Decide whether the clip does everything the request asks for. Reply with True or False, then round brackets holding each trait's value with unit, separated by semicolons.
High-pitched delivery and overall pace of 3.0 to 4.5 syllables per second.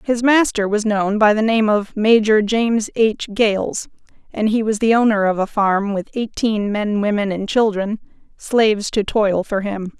True (215 Hz; 4.4 syllables/s)